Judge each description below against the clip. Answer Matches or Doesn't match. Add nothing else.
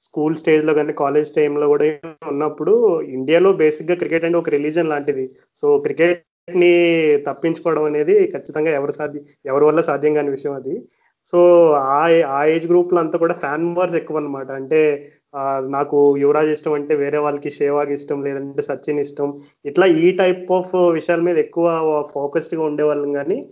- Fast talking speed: Matches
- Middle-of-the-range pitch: Matches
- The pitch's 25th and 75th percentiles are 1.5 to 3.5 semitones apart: Matches